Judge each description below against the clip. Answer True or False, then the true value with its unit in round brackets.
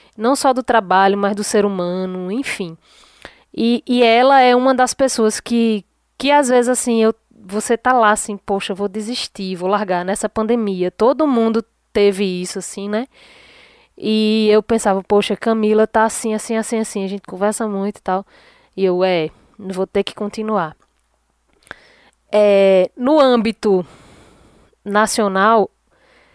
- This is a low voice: False (215 Hz)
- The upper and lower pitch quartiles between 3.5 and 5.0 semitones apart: False (2.9 semitones)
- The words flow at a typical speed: True (150 wpm)